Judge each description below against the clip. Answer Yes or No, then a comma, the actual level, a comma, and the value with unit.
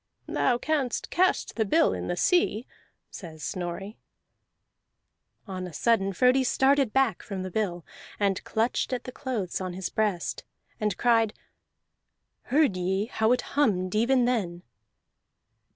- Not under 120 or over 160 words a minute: Yes, slow, 135 wpm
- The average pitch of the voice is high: Yes, high, 215 Hz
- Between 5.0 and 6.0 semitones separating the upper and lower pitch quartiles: Yes, average, 5.3 semitones